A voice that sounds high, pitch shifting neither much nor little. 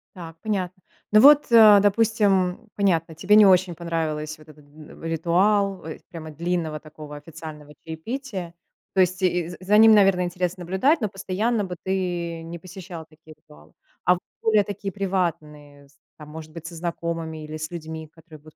No: medium, 175 Hz; average, 3.5 semitones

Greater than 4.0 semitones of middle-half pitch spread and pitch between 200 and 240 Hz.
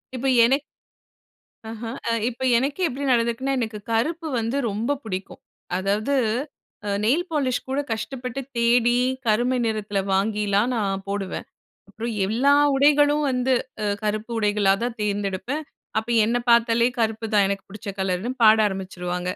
No: average, 3.6 semitones; high, 225 Hz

